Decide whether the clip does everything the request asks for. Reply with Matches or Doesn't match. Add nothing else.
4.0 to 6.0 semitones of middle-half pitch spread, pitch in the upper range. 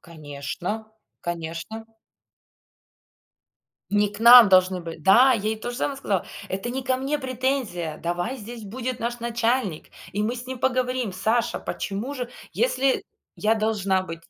Matches